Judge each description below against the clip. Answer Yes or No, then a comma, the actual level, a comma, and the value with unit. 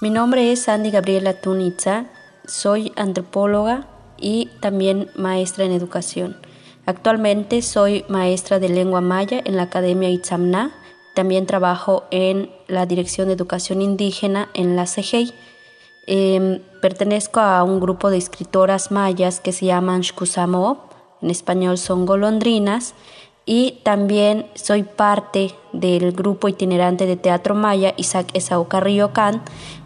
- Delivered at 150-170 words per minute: No, average, 130 wpm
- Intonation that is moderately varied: No, narrow, 2.1 semitones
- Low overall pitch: No, high, 190 Hz